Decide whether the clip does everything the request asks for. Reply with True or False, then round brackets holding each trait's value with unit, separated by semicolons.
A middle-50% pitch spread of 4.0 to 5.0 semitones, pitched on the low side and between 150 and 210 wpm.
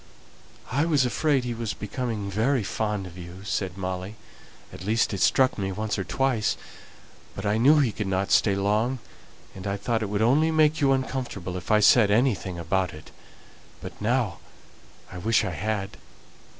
True (4.4 semitones; 105 Hz; 175 wpm)